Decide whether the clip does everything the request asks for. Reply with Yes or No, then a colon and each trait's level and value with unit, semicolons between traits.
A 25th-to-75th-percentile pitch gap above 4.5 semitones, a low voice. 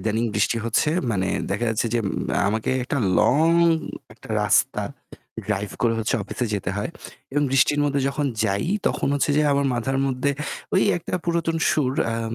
Yes: average, 4.9 semitones; low, 125 Hz